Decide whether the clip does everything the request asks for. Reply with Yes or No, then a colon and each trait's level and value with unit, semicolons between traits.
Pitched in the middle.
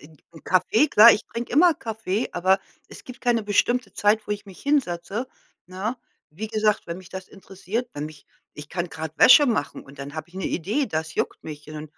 No: high, 195 Hz